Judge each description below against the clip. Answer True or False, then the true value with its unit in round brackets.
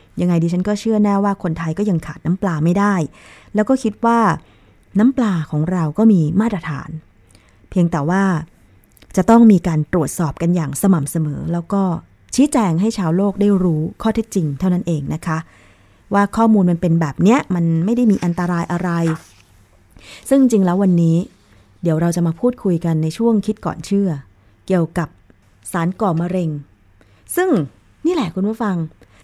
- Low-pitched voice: False (175 Hz)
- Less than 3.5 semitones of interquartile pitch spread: False (4.8 semitones)